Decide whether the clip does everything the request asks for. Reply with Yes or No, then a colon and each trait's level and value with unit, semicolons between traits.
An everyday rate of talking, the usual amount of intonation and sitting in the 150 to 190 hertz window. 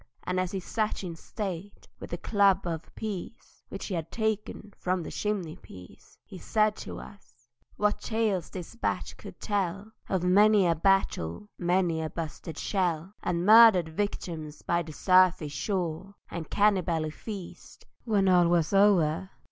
Yes: average, 155 wpm; average, 3.5 semitones; medium, 185 Hz